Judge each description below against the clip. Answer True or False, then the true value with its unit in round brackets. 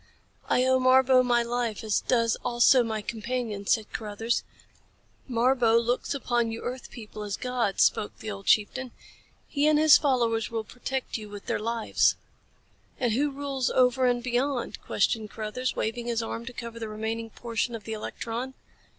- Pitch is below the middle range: False (235 Hz)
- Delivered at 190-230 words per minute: False (170 wpm)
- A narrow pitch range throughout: True (2.3 semitones)